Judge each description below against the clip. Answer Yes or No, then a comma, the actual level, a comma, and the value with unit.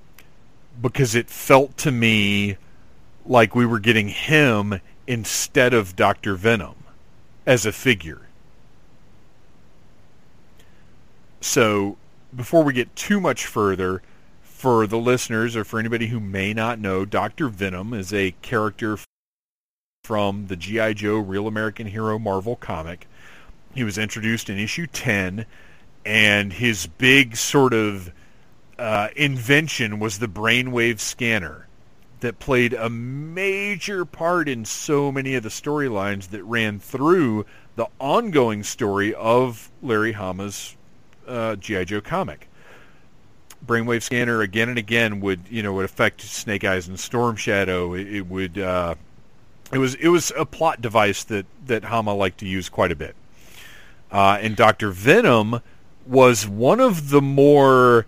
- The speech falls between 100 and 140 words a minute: Yes, slow, 135 wpm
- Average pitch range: Yes, average, 3.7 semitones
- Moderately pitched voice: No, low, 110 Hz